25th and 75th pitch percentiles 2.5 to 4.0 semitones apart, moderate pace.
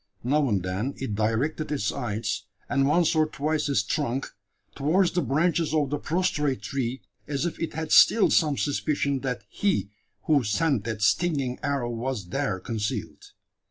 No: average, 5.0 semitones; average, 160 wpm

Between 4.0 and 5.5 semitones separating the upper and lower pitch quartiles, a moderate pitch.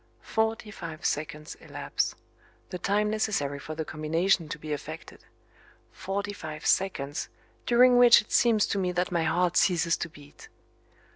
Yes: average, 4.8 semitones; medium, 175 Hz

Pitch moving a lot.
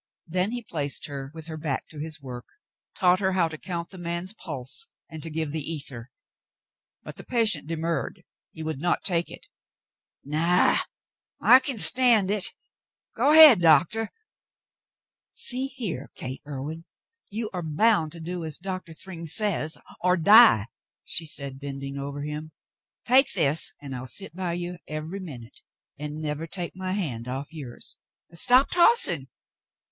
No: average, 4.3 semitones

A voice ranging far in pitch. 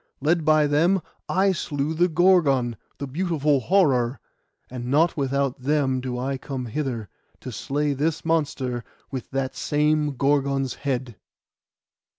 No: average, 2.9 semitones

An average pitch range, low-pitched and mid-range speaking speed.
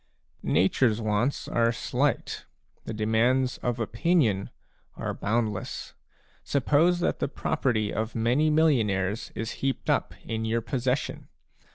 No: average, 3.7 semitones; low, 115 Hz; slow, 115 wpm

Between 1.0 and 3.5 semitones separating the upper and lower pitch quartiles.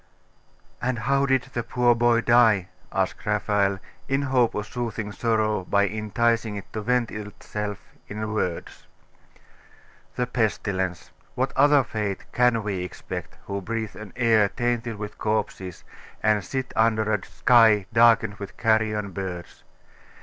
Yes: narrow, 2.6 semitones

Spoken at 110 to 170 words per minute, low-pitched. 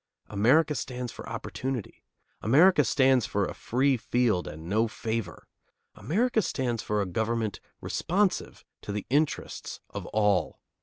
Yes: slow, 135 wpm; low, 120 Hz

